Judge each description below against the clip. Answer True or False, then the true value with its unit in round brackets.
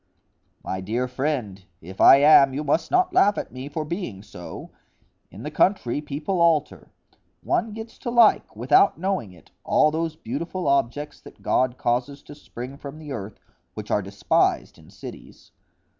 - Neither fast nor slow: True (165 wpm)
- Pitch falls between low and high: True (145 Hz)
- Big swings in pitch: True (5.7 semitones)